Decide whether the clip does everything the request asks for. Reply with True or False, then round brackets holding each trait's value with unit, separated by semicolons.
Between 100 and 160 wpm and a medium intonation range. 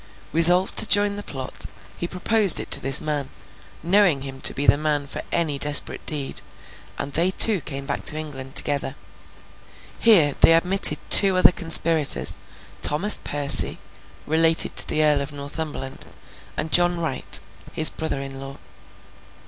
True (155 wpm; 3.9 semitones)